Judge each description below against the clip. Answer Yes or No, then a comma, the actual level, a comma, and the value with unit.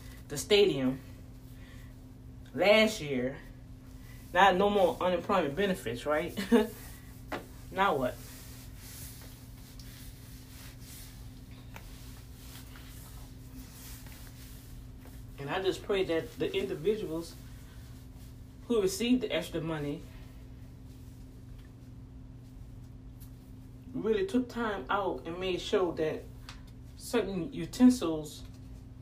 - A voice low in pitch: Yes, low, 130 Hz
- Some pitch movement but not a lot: No, wide, 6.8 semitones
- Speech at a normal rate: No, slow, 70 wpm